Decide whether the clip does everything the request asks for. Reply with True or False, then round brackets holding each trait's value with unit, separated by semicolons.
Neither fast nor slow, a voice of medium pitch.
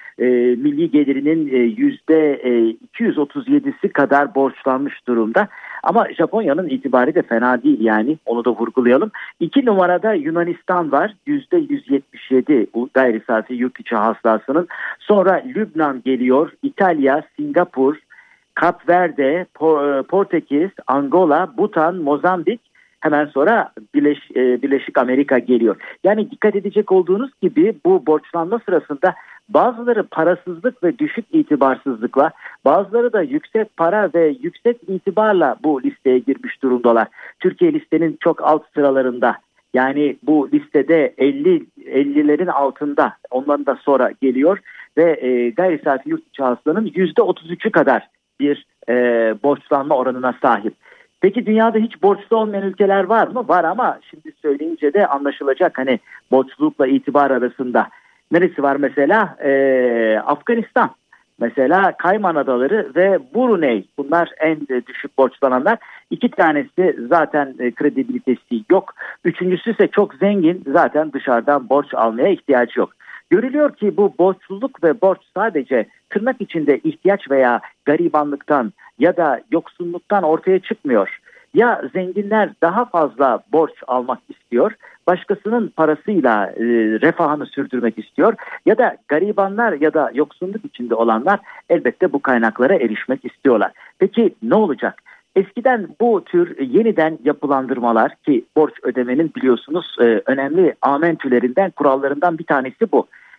True (120 wpm; 160 Hz)